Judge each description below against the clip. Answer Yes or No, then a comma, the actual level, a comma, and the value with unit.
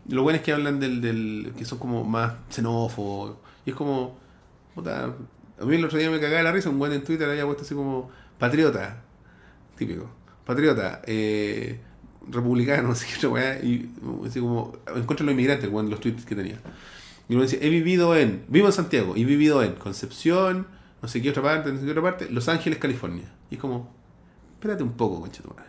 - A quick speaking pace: Yes, fast, 205 wpm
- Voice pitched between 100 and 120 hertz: No, low, 130 Hz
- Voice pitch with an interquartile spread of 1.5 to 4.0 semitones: No, average, 4.4 semitones